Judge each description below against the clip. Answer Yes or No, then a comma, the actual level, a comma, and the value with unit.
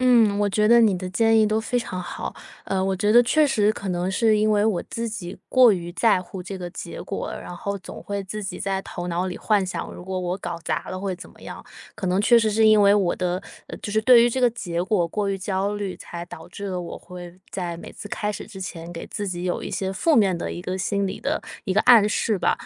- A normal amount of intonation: Yes, average, 3.0 semitones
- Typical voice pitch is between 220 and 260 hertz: No, high, 195 Hz